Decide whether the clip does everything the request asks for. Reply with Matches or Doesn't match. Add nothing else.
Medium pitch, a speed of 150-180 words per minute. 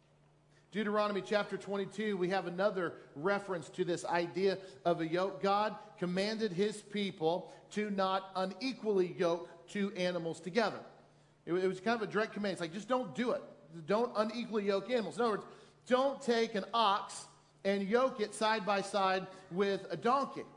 Doesn't match